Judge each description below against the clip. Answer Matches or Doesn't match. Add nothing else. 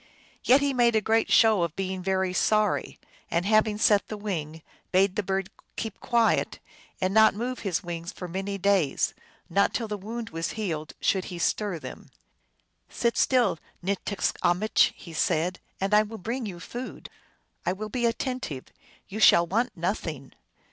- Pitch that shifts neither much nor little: Matches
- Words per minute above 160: Matches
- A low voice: Doesn't match